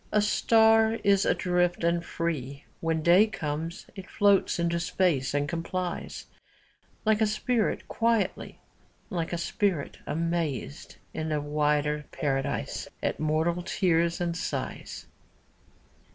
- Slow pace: Yes, slow, 125 wpm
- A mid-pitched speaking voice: Yes, medium, 170 Hz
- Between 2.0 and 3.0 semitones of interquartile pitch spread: No, average, 4.2 semitones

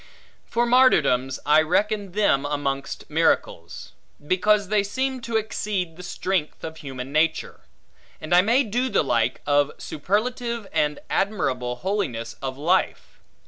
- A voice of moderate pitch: Yes, medium, 180 Hz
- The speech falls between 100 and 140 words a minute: Yes, slow, 135 wpm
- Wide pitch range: Yes, wide, 6.8 semitones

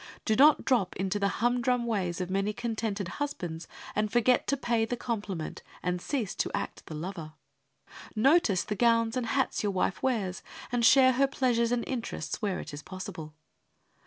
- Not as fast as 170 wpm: No, average, 175 wpm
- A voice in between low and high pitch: No, high, 225 Hz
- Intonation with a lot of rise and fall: No, average, 4.5 semitones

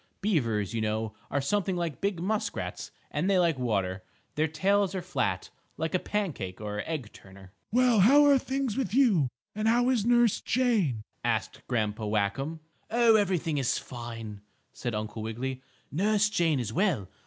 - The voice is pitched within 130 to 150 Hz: No, medium, 160 Hz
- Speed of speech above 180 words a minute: No, average, 165 wpm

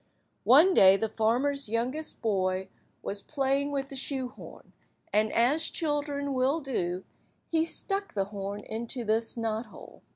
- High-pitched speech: Yes, high, 245 Hz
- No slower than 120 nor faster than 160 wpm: Yes, slow, 135 wpm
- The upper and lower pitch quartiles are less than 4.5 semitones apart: No, average, 4.9 semitones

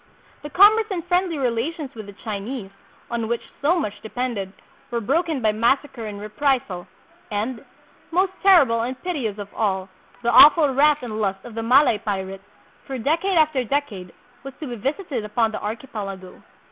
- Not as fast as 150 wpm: No, average, 170 wpm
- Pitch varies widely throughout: Yes, wide, 5.8 semitones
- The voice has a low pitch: No, high, 240 Hz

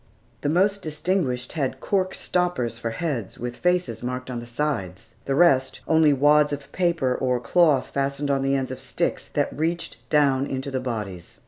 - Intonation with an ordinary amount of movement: Yes, average, 4.0 semitones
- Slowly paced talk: No, average, 180 wpm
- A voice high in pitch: No, low, 135 Hz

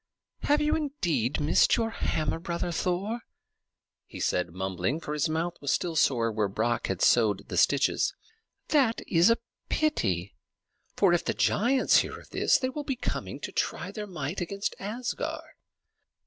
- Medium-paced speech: Yes, average, 160 wpm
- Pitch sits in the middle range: Yes, medium, 170 Hz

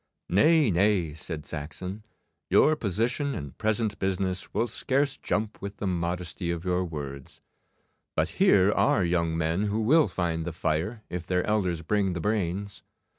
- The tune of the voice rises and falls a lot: No, average, 4.1 semitones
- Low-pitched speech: Yes, very low, 95 Hz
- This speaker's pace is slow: No, average, 155 wpm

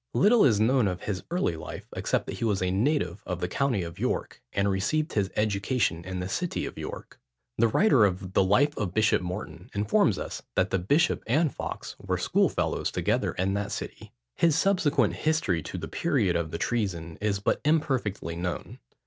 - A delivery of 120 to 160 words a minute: No, average, 190 wpm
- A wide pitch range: Yes, wide, 7.0 semitones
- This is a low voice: Yes, low, 100 Hz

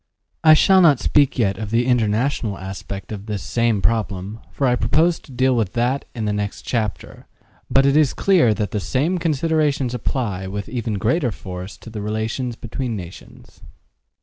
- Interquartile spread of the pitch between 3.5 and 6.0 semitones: Yes, average, 4.7 semitones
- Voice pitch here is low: Yes, low, 115 Hz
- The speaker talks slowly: No, average, 175 wpm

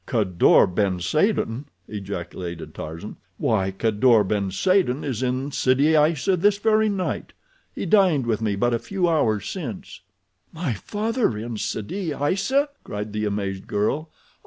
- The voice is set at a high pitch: No, low, 120 Hz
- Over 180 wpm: No, average, 140 wpm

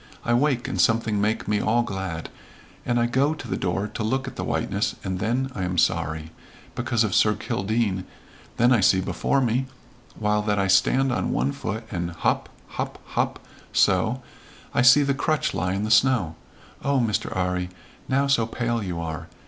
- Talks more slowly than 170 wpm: No, average, 190 wpm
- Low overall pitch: Yes, low, 110 Hz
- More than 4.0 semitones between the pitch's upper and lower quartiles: Yes, average, 4.7 semitones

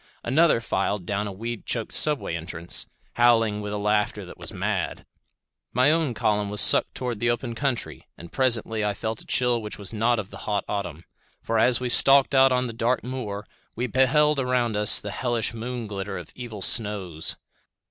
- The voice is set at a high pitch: No, low, 115 Hz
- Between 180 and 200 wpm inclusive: Yes, average, 190 wpm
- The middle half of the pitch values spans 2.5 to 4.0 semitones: Yes, average, 3.4 semitones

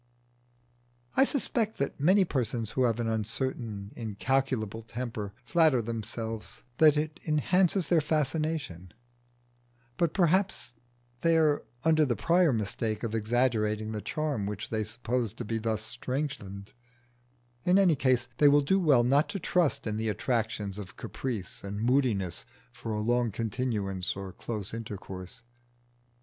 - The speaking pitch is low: Yes, low, 120 Hz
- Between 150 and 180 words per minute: No, average, 140 wpm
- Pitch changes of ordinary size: No, wide, 5.8 semitones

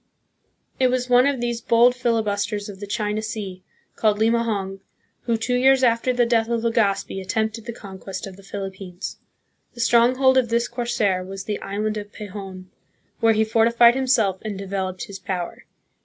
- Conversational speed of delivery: Yes, average, 170 wpm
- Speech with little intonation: No, average, 3.3 semitones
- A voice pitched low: No, high, 220 Hz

